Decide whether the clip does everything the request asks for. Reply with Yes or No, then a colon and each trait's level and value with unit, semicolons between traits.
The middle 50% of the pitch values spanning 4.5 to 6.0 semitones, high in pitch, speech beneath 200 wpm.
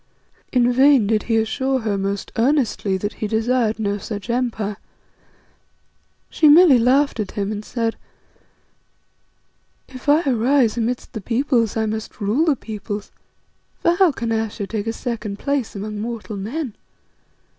No: average, 3.5 semitones; high, 225 Hz; average, 145 wpm